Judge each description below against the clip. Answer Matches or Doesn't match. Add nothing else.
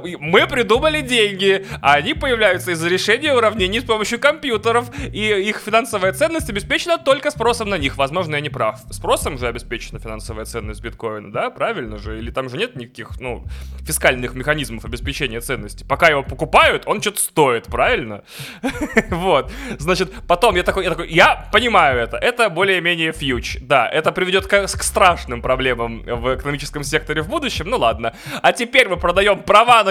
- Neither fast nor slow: Doesn't match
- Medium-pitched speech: Matches